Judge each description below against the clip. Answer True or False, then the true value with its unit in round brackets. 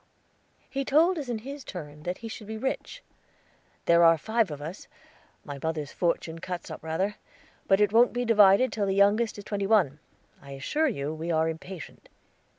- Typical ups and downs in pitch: False (5.9 semitones)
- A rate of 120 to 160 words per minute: False (185 wpm)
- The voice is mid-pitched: False (195 Hz)